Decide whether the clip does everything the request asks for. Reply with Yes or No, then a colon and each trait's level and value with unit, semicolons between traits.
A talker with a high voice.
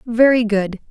Yes: high, 225 Hz